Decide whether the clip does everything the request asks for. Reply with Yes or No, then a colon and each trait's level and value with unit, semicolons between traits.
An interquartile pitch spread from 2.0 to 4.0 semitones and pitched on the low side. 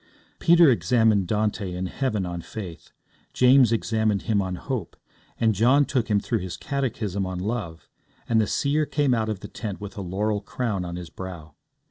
No: average, 4.6 semitones; low, 110 Hz